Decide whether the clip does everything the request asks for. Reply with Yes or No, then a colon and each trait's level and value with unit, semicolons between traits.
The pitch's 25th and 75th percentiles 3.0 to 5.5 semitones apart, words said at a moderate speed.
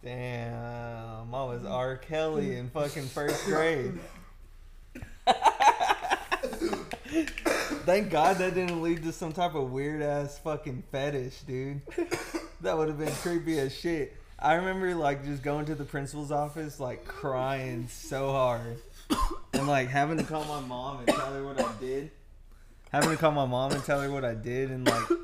Yes: average, 3.9 semitones; average, 165 wpm